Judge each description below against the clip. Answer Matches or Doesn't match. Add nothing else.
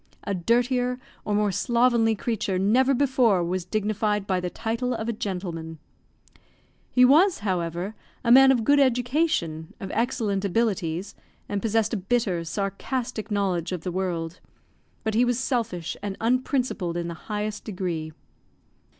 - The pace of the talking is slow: Doesn't match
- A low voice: Doesn't match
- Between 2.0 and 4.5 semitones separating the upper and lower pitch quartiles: Doesn't match